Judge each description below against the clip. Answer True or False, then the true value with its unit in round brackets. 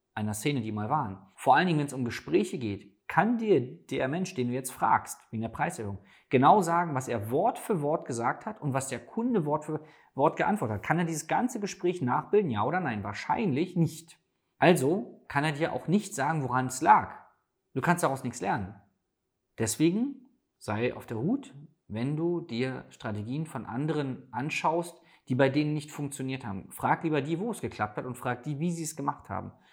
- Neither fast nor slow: False (205 wpm)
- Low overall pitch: False (145 Hz)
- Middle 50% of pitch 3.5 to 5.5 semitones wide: True (5.1 semitones)